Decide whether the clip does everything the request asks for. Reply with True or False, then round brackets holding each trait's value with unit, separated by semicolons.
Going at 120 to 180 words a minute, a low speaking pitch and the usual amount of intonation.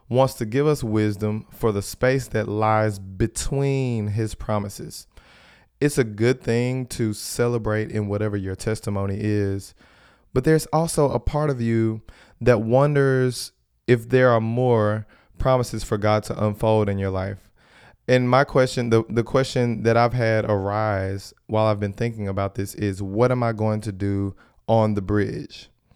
True (165 wpm; 110 Hz; 3.1 semitones)